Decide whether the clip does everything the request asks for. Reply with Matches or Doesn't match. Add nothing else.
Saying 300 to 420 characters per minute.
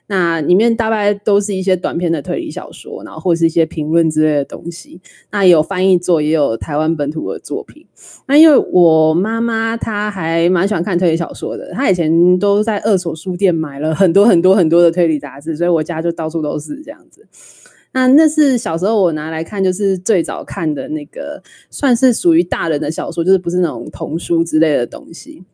Matches